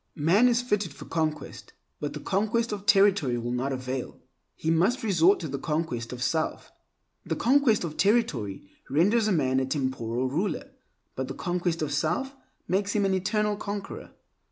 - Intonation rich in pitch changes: Yes, wide, 7.3 semitones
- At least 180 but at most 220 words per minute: No, average, 165 wpm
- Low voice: No, medium, 170 Hz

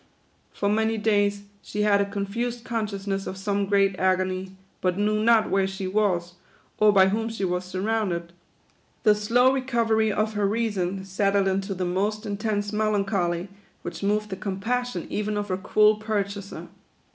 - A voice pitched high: Yes, high, 205 Hz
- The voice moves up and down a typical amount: No, narrow, 2.0 semitones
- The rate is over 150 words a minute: Yes, average, 160 wpm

